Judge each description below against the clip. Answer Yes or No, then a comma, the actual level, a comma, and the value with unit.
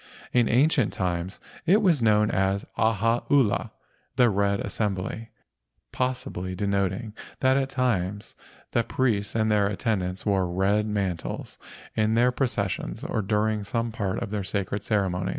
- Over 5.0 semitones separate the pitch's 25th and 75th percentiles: No, average, 3.2 semitones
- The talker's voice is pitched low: Yes, low, 105 Hz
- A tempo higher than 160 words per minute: No, average, 140 wpm